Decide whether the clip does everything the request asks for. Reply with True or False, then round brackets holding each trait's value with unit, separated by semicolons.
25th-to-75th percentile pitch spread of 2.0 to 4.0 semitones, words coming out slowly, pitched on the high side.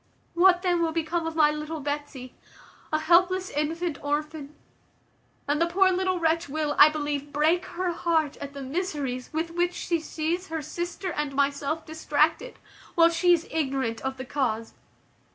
False (3.0 semitones; 165 wpm; 315 Hz)